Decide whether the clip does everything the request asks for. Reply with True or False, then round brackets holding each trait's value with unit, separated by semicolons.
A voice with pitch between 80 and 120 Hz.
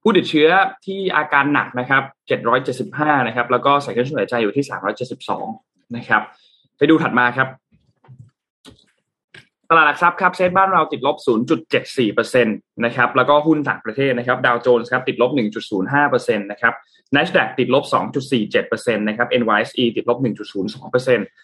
False (140 Hz)